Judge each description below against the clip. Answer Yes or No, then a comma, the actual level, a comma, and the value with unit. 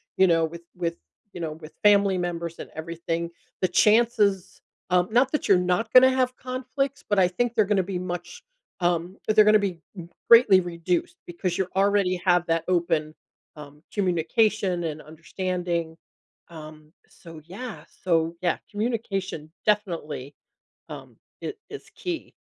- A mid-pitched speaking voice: Yes, medium, 180 Hz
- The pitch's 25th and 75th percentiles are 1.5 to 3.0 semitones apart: No, average, 3.7 semitones